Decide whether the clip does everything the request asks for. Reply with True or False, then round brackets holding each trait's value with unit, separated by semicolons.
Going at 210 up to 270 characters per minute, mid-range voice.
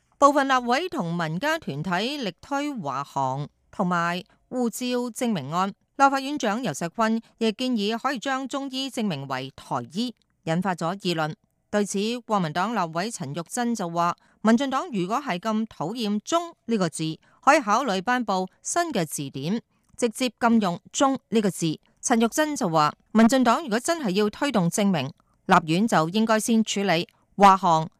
False (250 characters per minute; 215 Hz)